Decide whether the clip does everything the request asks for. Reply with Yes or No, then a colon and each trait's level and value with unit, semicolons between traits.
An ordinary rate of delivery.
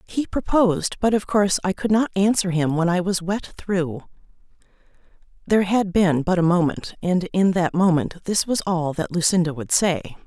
Yes: average, 185 wpm